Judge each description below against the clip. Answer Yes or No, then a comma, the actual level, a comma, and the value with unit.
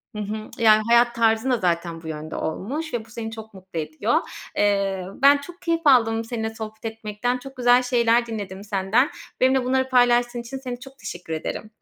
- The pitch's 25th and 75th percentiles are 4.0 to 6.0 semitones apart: No, average, 3.4 semitones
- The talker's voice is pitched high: Yes, high, 225 Hz